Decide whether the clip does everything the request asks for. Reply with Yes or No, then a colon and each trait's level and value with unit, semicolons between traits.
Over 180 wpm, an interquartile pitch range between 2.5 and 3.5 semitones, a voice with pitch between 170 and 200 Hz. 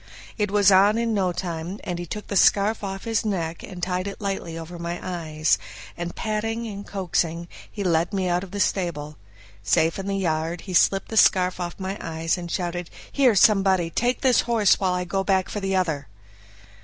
Yes: fast, 205 wpm; average, 2.8 semitones; medium, 185 Hz